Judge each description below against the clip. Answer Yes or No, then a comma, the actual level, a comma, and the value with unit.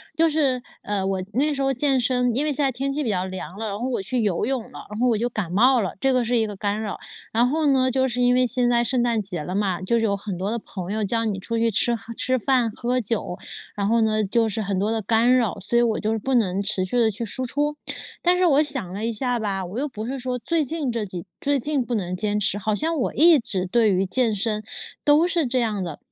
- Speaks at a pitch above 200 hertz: Yes, high, 230 Hz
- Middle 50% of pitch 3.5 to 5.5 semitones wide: Yes, average, 3.9 semitones